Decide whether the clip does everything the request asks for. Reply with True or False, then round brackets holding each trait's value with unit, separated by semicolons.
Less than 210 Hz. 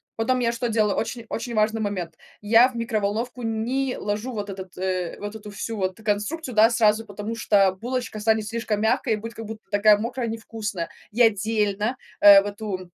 False (220 Hz)